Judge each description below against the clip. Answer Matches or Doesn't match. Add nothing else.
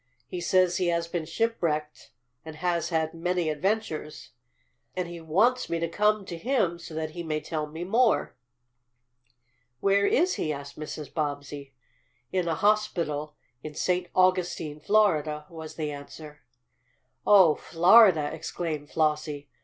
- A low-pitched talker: Doesn't match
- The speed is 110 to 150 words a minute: Matches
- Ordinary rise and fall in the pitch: Matches